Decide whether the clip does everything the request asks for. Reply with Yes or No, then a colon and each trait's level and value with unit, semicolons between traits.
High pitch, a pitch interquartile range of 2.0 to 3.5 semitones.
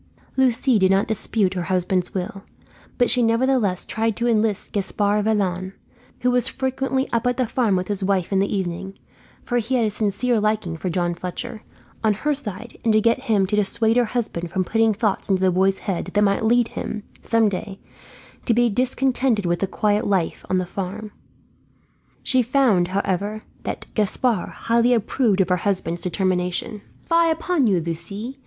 No: high, 210 Hz; average, 3.9 semitones